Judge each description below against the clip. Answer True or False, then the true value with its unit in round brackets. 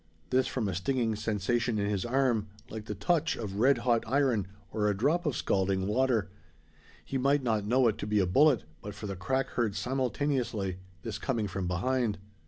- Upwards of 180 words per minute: True (190 wpm)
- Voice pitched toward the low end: True (115 Hz)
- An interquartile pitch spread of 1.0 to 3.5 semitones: False (4.4 semitones)